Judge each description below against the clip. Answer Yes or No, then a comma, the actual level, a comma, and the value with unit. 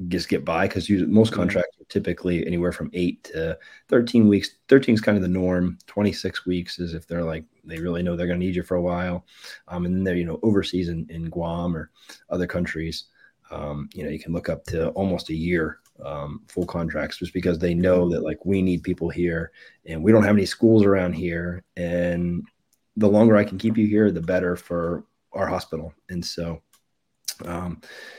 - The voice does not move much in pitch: Yes, narrow, 1.8 semitones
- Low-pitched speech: Yes, very low, 90 Hz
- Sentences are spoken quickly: Yes, fast, 210 wpm